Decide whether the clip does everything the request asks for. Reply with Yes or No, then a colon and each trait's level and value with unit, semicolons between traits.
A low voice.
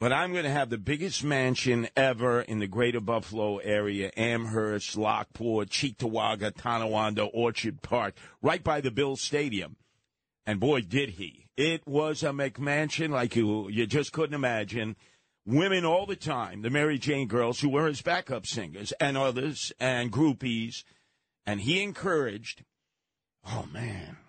Yes: low, 125 Hz